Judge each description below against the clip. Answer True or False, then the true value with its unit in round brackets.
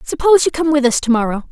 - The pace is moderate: False (240 wpm)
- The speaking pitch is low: False (275 Hz)